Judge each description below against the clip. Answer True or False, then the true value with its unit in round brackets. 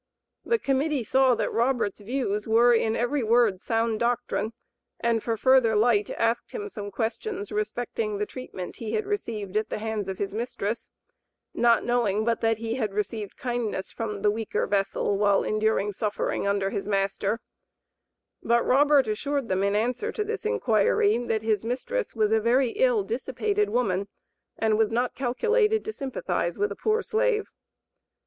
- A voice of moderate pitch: False (230 Hz)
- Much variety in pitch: False (4.1 semitones)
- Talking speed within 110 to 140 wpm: False (165 wpm)